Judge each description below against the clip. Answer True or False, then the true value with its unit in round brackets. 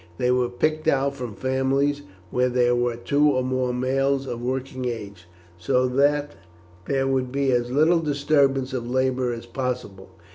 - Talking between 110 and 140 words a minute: False (160 wpm)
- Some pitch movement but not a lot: False (2.0 semitones)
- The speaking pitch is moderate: False (130 Hz)